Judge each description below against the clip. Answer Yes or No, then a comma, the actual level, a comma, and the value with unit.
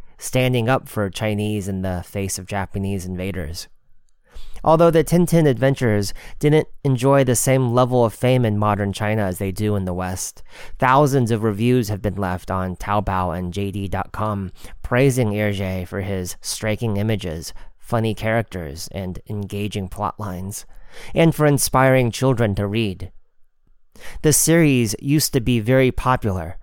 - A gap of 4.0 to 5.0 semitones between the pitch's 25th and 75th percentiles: Yes, average, 4.6 semitones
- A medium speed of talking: Yes, average, 145 wpm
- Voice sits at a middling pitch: No, low, 105 Hz